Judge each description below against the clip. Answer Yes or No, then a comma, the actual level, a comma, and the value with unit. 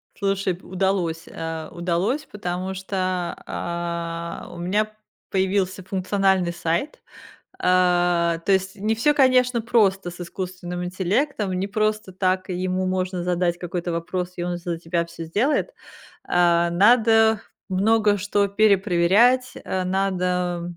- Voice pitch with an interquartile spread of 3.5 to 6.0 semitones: No, narrow, 2.6 semitones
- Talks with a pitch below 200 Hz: Yes, medium, 185 Hz